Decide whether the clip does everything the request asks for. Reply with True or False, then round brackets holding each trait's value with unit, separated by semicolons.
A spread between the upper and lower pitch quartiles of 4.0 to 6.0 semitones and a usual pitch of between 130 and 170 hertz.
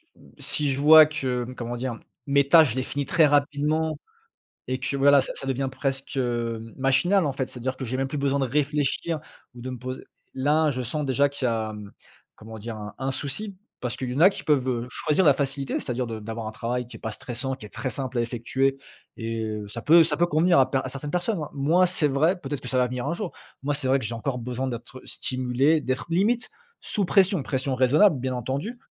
False (3.1 semitones; 135 Hz)